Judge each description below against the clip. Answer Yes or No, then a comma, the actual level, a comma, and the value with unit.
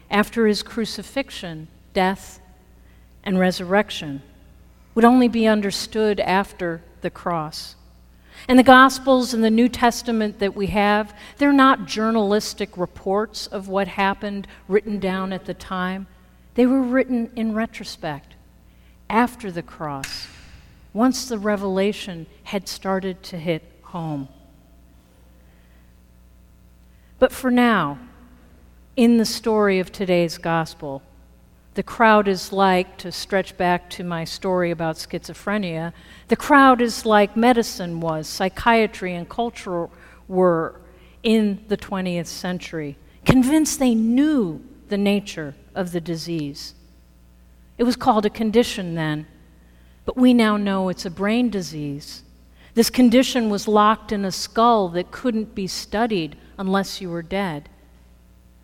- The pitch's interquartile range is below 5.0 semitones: No, average, 5.3 semitones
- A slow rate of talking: Yes, slow, 125 wpm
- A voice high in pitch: Yes, high, 195 Hz